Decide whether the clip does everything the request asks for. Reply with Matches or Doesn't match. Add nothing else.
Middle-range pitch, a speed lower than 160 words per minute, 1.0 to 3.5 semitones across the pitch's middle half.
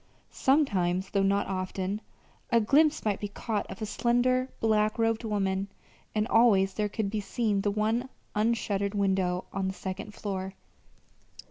Doesn't match